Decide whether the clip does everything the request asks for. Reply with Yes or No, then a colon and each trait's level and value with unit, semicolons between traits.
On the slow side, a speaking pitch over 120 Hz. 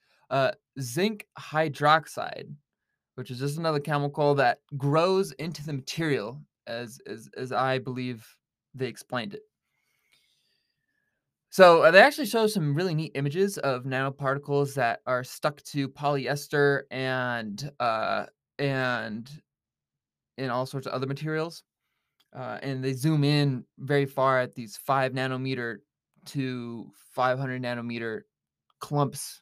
Yes: slow, 125 wpm; medium, 140 Hz